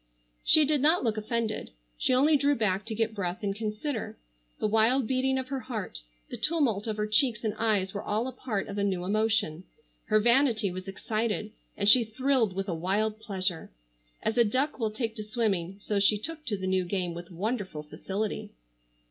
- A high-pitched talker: Yes, high, 215 Hz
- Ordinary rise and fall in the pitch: Yes, average, 3.5 semitones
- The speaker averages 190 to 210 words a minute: Yes, average, 200 wpm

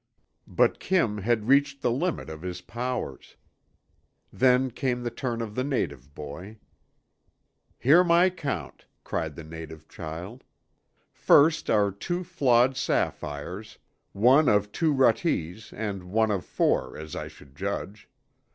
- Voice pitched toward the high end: No, low, 110 Hz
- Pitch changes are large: Yes, wide, 6.8 semitones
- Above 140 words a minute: No, slow, 135 wpm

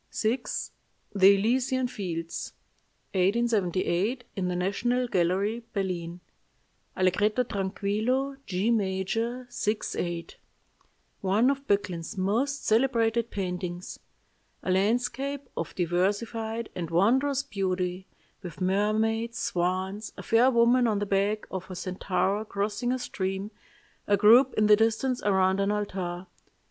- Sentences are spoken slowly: Yes, slow, 115 wpm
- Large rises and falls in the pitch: No, average, 3.9 semitones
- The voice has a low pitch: No, high, 205 Hz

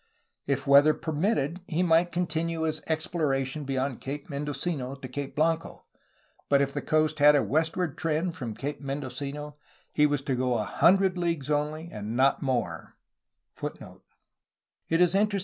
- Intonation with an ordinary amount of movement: Yes, average, 3.0 semitones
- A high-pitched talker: No, medium, 150 Hz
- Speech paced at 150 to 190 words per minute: No, average, 140 wpm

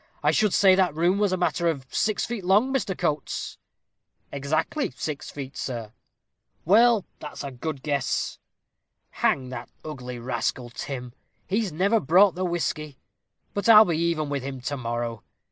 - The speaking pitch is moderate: Yes, medium, 155 Hz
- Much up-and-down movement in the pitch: Yes, wide, 6.2 semitones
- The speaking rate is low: No, average, 160 wpm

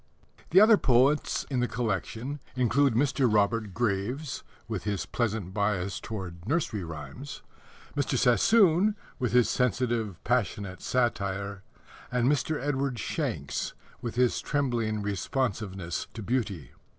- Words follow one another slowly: Yes, slow, 120 wpm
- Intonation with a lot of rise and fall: No, average, 4.6 semitones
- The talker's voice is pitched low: Yes, low, 120 Hz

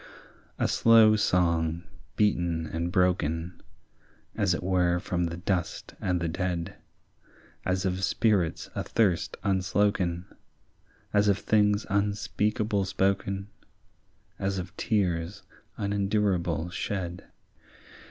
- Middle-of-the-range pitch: No, very low, 95 Hz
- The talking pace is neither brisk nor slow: No, slow, 100 wpm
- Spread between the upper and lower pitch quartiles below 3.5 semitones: Yes, average, 2.8 semitones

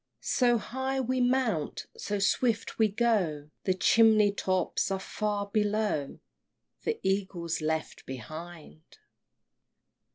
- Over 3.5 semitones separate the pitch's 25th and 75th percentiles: Yes, average, 5.2 semitones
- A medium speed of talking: No, slow, 105 wpm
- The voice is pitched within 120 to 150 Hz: No, high, 205 Hz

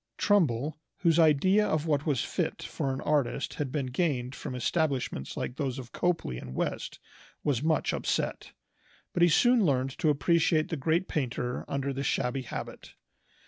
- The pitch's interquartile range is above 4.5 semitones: No, average, 4.0 semitones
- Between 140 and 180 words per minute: Yes, average, 165 wpm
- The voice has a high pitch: No, medium, 145 Hz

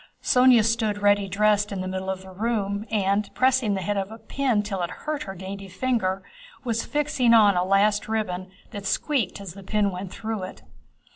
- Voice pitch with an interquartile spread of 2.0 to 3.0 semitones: Yes, average, 2.7 semitones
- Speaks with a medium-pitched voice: No, high, 205 Hz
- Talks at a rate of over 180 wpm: Yes, average, 200 wpm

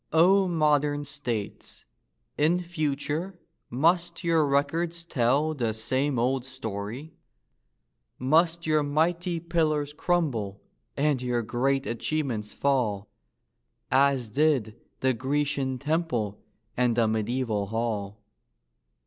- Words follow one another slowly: Yes, slow, 100 wpm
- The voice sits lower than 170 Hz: Yes, medium, 140 Hz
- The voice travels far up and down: No, average, 4.8 semitones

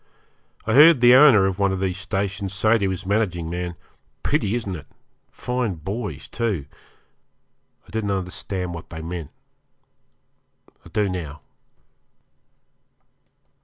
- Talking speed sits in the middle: No, slow, 130 wpm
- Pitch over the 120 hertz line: No, very low, 95 Hz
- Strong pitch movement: No, average, 3.4 semitones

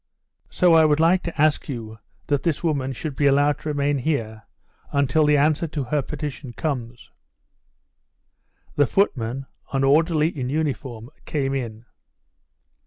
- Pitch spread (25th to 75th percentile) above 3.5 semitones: No, average, 3.0 semitones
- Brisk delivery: No, average, 145 wpm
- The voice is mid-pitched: Yes, medium, 145 Hz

